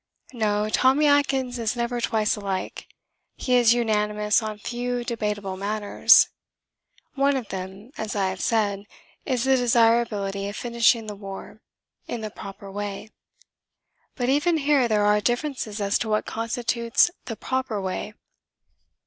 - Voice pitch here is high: Yes, high, 220 Hz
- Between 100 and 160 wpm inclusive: Yes, average, 140 wpm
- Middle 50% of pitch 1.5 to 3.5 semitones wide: Yes, average, 3.0 semitones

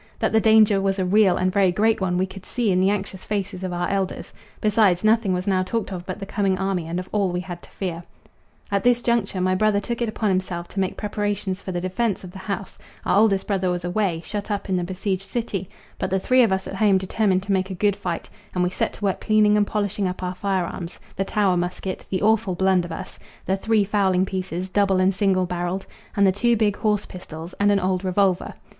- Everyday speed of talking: No, fast, 240 wpm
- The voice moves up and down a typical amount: No, narrow, 2.0 semitones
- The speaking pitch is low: No, high, 190 Hz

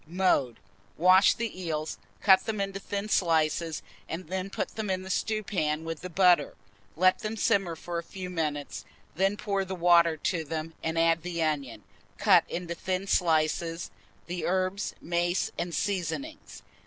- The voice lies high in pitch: No, medium, 175 Hz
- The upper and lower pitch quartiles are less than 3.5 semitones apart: Yes, average, 2.8 semitones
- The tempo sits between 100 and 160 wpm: Yes, average, 155 wpm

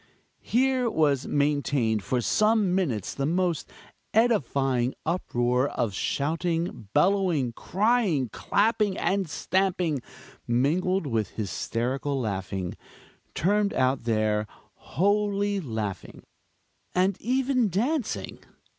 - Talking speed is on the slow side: Yes, slow, 95 wpm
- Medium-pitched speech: Yes, medium, 160 Hz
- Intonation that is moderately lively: No, wide, 8.4 semitones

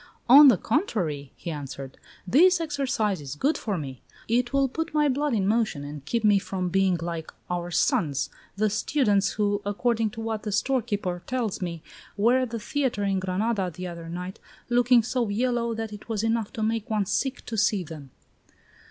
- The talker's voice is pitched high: Yes, high, 210 Hz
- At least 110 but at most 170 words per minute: No, average, 185 wpm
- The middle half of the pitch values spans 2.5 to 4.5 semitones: No, average, 5.0 semitones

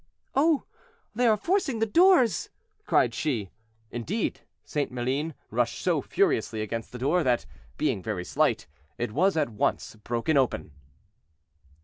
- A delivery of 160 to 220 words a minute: No, slow, 135 wpm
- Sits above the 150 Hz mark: No, medium, 140 Hz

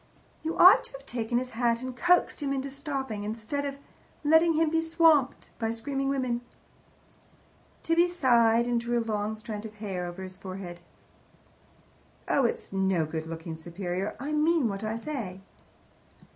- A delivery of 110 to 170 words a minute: Yes, average, 160 wpm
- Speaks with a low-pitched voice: No, high, 235 Hz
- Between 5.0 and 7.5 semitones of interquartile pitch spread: Yes, wide, 5.6 semitones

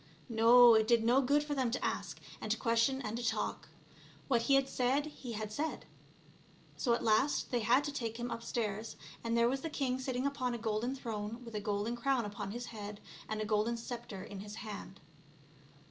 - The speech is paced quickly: Yes, fast, 210 wpm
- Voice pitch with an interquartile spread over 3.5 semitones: No, average, 3.0 semitones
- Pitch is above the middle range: Yes, high, 235 Hz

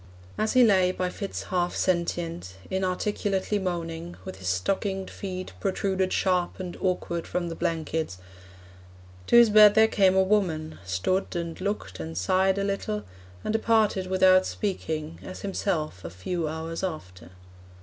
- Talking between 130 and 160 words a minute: Yes, average, 150 wpm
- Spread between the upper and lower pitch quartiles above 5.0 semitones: No, average, 3.1 semitones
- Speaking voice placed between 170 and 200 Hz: Yes, medium, 185 Hz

